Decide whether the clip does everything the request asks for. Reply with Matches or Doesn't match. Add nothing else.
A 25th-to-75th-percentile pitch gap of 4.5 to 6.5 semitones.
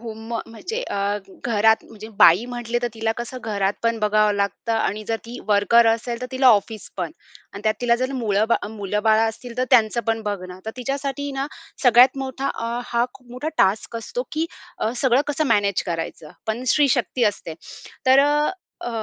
Doesn't match